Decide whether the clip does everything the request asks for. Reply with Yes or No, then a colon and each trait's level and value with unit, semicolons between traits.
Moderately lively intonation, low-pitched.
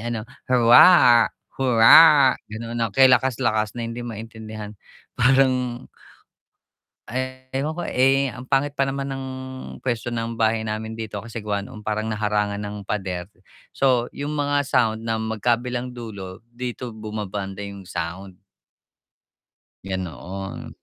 Yes: average, 3.3 semitones; low, 115 Hz